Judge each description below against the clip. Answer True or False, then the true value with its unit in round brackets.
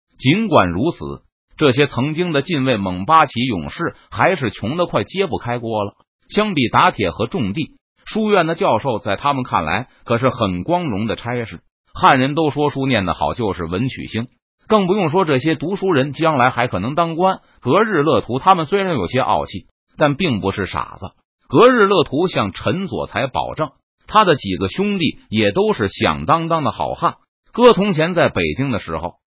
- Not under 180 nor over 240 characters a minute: False (270 characters per minute)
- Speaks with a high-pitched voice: False (135 Hz)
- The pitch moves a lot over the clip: True (7.2 semitones)